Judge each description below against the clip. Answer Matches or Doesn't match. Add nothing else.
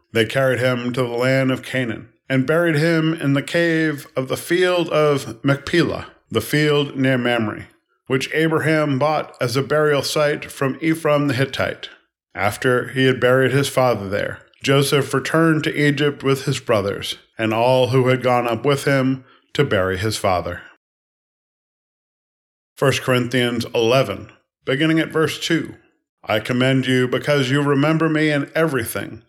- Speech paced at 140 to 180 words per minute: Matches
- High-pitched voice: Doesn't match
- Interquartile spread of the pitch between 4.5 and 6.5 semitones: Doesn't match